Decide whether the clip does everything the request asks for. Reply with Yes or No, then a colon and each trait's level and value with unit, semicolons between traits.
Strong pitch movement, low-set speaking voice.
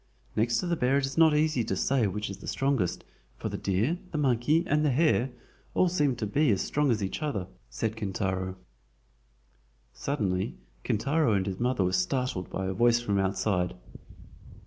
Yes: wide, 6.8 semitones; low, 120 Hz